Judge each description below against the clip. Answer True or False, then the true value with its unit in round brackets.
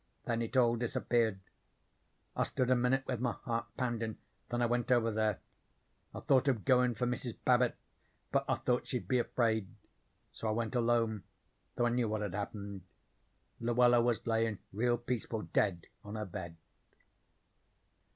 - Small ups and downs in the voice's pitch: True (2.0 semitones)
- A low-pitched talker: True (115 Hz)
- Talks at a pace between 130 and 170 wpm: True (160 wpm)